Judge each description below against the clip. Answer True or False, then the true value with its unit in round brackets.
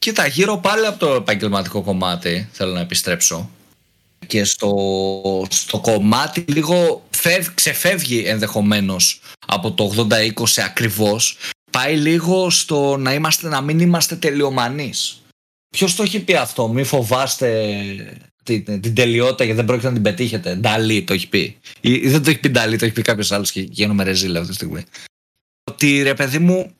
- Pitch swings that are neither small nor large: False (6.8 semitones)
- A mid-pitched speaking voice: False (115 Hz)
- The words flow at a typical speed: True (160 wpm)